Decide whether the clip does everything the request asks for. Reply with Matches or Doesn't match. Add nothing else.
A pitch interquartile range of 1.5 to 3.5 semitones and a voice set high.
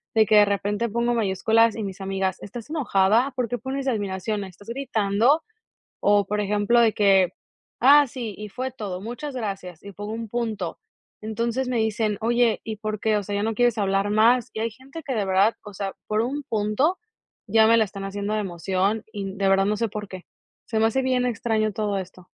Matches